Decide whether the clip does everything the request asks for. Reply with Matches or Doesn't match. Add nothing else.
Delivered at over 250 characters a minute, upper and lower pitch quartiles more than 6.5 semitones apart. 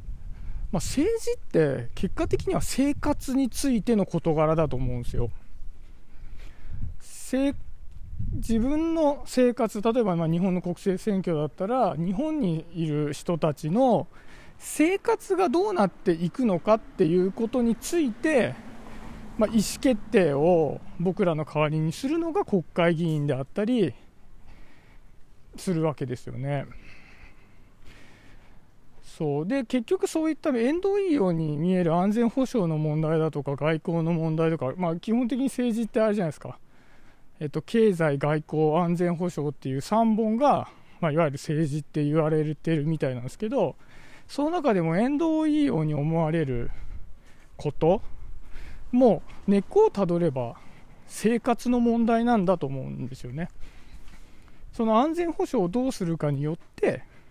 Matches